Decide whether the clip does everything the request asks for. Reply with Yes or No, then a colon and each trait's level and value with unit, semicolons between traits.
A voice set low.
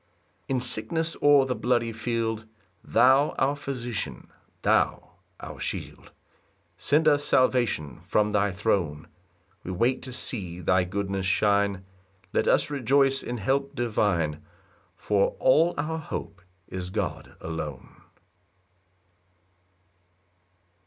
Yes: low, 115 Hz